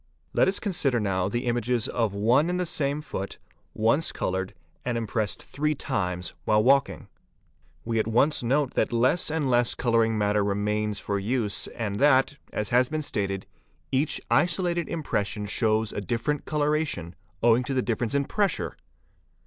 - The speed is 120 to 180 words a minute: Yes, average, 160 wpm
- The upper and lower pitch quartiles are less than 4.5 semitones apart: No, wide, 5.4 semitones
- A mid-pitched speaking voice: No, low, 120 Hz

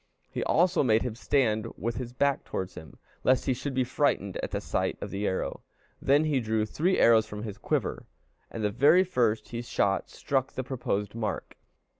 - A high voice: No, low, 120 Hz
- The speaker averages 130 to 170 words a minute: No, average, 195 wpm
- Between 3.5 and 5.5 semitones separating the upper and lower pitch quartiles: Yes, average, 4.3 semitones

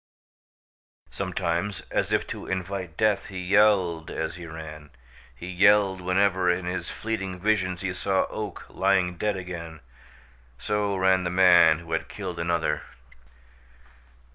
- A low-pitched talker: Yes, very low, 90 Hz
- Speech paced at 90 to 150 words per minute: Yes, slow, 135 wpm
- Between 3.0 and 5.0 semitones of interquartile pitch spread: No, narrow, 2.4 semitones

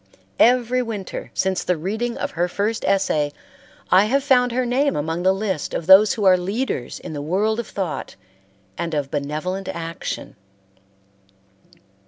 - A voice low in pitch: No, high, 195 Hz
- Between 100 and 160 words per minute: Yes, average, 155 wpm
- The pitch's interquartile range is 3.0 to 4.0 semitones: No, wide, 5.5 semitones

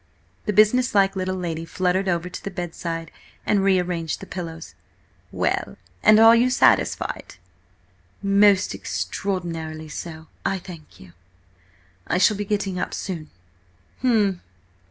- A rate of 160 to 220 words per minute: No, slow, 135 wpm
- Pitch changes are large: No, average, 3.2 semitones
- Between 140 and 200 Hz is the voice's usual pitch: Yes, medium, 185 Hz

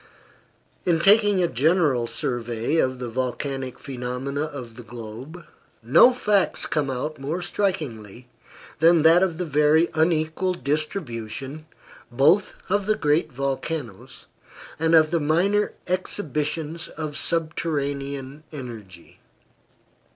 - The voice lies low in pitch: No, medium, 150 Hz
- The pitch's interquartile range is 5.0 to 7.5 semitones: No, average, 4.6 semitones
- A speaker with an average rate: No, slow, 115 wpm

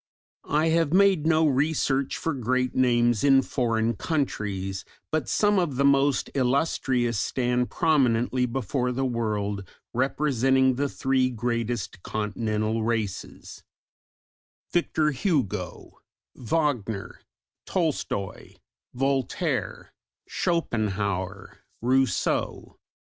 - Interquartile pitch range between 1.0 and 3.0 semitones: No, average, 4.2 semitones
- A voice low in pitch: Yes, low, 125 Hz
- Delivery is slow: Yes, slow, 90 wpm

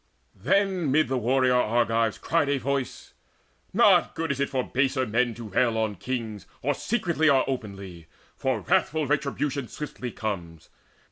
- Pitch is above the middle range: No, low, 130 Hz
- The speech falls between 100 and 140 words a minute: No, average, 150 wpm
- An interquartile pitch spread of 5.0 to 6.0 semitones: No, average, 4.2 semitones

